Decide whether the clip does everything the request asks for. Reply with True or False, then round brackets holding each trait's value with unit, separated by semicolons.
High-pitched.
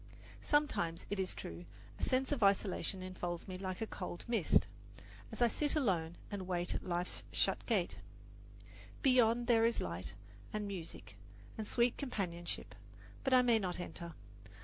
True (195 Hz)